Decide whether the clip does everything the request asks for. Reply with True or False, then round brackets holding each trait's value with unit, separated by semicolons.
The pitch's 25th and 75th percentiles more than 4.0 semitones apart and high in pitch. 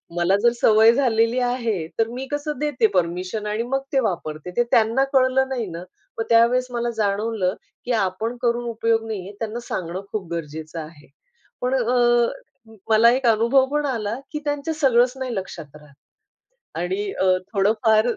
True (4.5 semitones; 230 Hz)